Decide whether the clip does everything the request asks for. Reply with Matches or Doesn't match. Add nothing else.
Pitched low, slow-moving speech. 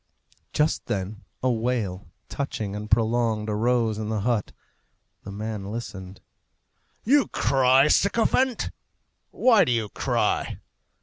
Matches